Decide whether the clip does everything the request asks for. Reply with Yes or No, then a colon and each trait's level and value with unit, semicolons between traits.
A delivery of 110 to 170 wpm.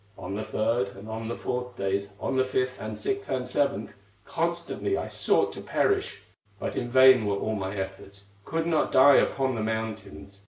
No: average, 190 wpm